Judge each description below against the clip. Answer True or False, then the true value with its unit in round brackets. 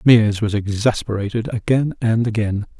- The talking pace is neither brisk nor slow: False (130 wpm)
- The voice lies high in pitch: False (110 Hz)